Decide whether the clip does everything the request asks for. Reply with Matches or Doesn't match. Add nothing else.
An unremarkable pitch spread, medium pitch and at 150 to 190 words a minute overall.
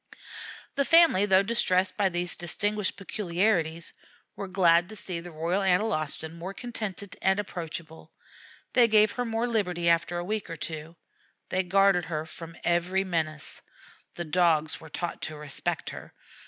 Matches